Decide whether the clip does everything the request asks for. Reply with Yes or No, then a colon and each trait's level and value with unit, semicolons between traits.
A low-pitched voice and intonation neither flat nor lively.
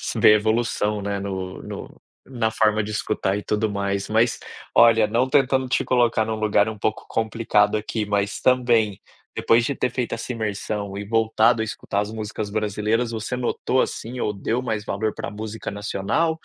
No: low, 110 Hz; narrow, 2.1 semitones